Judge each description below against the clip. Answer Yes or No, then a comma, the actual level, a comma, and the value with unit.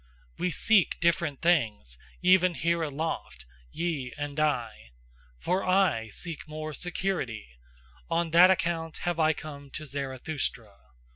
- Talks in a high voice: No, medium, 155 Hz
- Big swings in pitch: No, average, 4.7 semitones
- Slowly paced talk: Yes, slow, 125 wpm